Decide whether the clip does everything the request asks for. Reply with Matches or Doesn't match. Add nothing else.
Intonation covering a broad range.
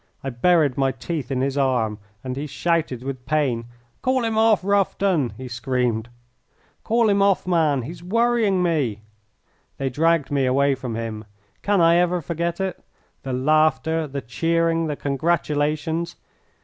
Doesn't match